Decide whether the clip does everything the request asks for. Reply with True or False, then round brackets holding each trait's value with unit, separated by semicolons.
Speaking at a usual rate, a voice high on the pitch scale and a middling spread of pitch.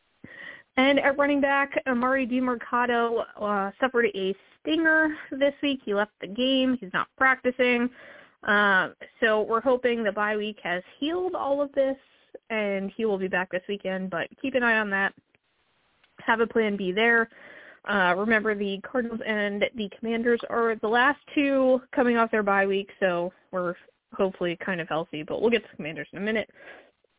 True (180 wpm; 230 Hz; 4.9 semitones)